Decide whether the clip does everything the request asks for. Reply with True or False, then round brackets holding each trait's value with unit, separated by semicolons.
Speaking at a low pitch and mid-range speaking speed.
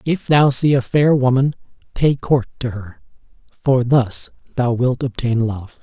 True (125 Hz; 165 wpm)